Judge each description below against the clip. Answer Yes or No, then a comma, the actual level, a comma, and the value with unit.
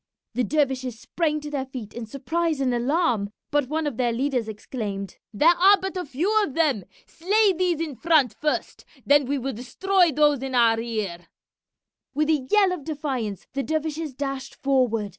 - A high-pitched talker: Yes, very high, 275 Hz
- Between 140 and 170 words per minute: No, average, 180 wpm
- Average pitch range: Yes, average, 4.8 semitones